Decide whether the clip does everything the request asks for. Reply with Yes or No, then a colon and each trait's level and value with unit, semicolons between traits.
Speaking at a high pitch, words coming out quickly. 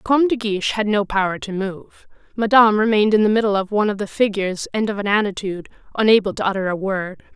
Yes: high, 205 Hz; fast, 230 wpm